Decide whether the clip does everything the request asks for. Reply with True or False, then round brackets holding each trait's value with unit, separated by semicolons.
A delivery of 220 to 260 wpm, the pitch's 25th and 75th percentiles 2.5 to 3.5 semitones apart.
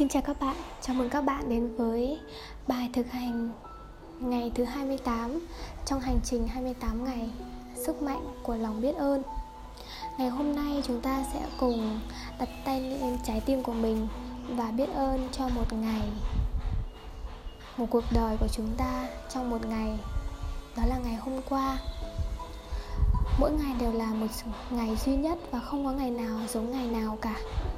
False (170 wpm; 3.1 semitones)